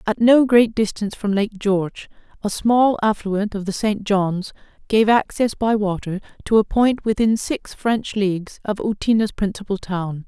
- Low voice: No, high, 210 Hz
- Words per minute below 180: Yes, average, 170 wpm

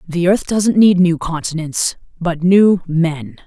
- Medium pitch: Yes, medium, 175 Hz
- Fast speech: No, average, 155 wpm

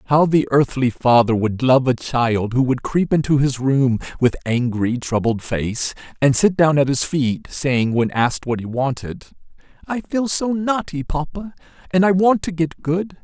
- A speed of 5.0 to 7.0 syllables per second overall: No, 4.4 syllables/s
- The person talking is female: No, male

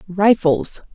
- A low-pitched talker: No, high, 200 Hz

